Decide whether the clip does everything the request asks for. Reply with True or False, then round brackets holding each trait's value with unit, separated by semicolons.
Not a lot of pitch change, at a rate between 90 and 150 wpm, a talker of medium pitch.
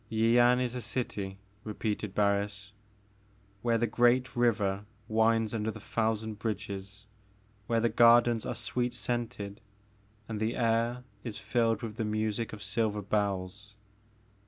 False (2.2 semitones; 135 wpm; 110 Hz)